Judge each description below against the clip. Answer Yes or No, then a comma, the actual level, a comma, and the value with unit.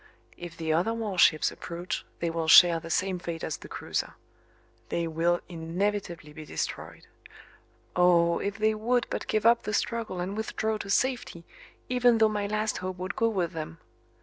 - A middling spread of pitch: Yes, average, 4.3 semitones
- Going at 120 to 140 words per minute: No, average, 175 wpm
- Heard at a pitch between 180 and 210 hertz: Yes, medium, 185 Hz